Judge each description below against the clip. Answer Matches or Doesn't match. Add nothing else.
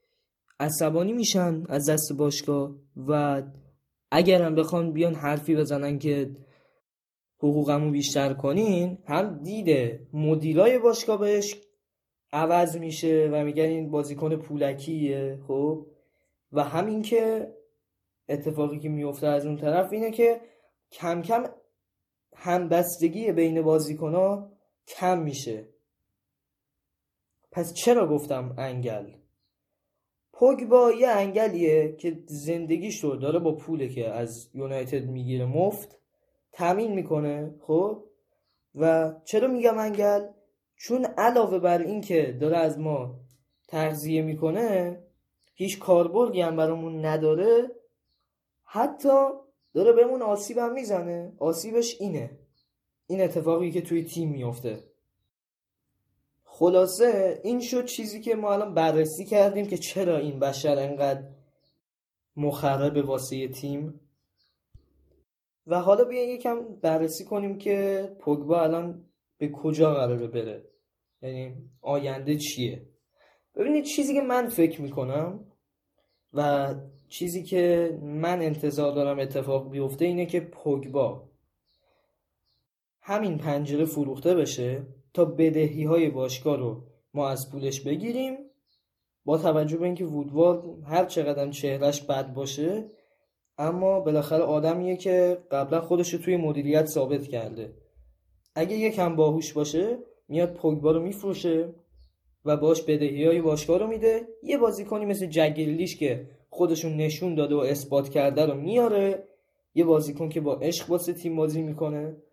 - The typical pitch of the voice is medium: Matches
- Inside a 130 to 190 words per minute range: Doesn't match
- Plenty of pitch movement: Doesn't match